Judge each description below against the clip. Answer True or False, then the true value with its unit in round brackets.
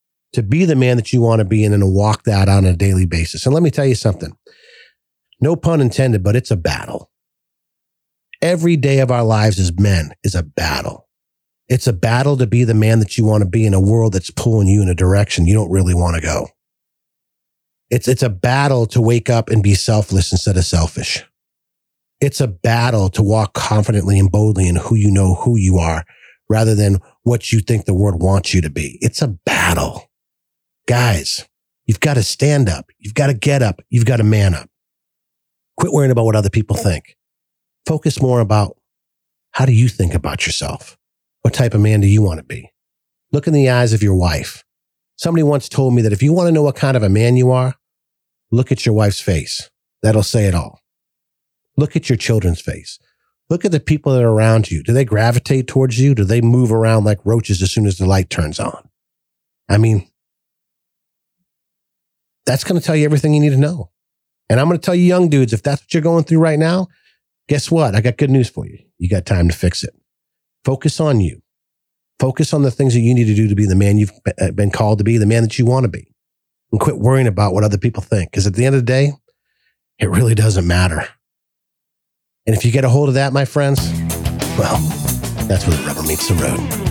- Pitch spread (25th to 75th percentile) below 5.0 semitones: False (5.3 semitones)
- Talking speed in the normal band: False (220 wpm)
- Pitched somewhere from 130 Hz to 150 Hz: False (115 Hz)